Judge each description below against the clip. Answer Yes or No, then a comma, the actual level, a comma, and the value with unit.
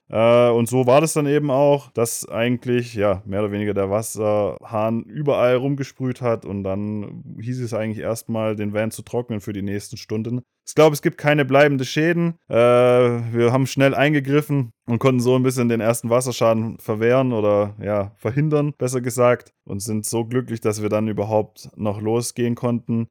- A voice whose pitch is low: Yes, low, 120 Hz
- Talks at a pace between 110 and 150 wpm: No, average, 175 wpm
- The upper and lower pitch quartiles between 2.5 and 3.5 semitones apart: Yes, average, 3.2 semitones